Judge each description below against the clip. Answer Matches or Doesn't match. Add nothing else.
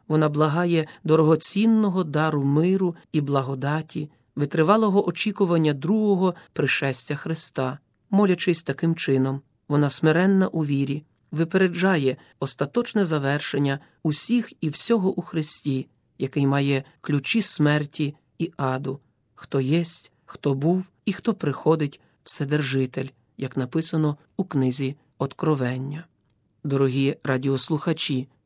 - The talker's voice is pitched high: Doesn't match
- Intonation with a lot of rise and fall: Doesn't match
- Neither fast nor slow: Doesn't match